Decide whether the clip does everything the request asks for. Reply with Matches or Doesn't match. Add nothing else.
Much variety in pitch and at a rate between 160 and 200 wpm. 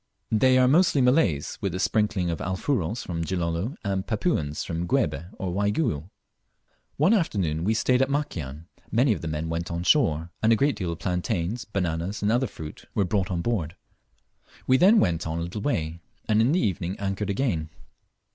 Matches